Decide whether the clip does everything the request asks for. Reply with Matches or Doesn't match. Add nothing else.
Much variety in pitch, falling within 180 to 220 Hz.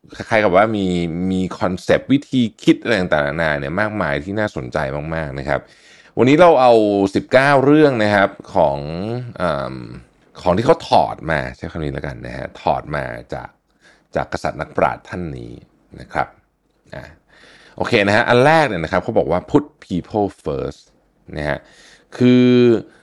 Doesn't match